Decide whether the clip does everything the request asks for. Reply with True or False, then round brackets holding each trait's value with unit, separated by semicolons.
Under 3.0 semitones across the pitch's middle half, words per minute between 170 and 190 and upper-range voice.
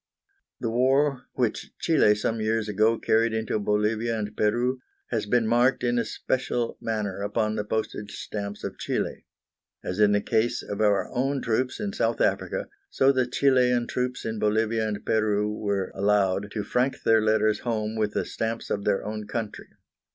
False (2.5 semitones; 175 wpm; 110 Hz)